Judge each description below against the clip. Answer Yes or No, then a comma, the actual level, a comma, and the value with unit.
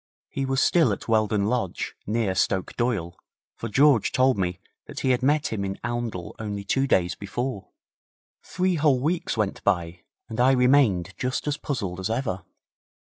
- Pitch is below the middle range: Yes, low, 115 Hz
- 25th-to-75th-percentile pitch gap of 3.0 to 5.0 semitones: No, wide, 5.4 semitones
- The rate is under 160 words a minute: No, average, 170 wpm